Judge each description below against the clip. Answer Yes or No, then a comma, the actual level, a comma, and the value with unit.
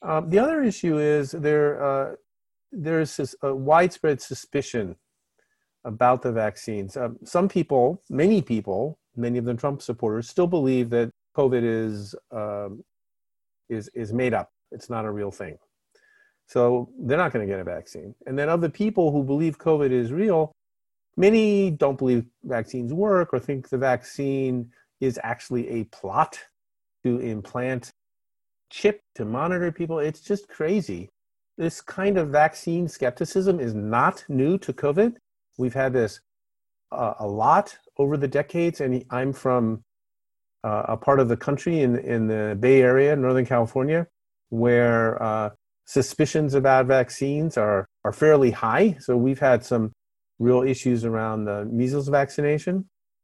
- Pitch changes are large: No, average, 4.9 semitones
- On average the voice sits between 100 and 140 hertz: Yes, low, 135 Hz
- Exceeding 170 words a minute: No, average, 150 wpm